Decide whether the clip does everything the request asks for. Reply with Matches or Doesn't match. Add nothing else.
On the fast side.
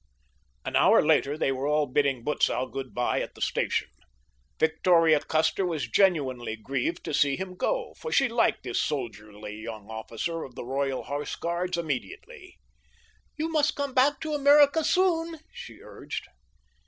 Doesn't match